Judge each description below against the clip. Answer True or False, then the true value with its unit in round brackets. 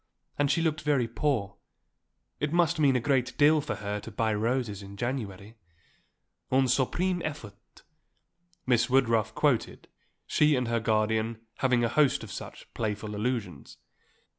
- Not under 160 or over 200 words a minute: False (145 wpm)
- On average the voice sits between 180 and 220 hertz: False (120 Hz)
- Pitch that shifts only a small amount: False (4.6 semitones)